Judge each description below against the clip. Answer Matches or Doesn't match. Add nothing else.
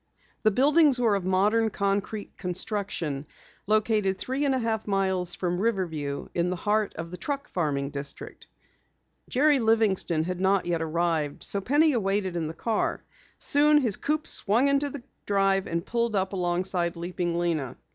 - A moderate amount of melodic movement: Matches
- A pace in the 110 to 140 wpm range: Doesn't match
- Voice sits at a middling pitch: Doesn't match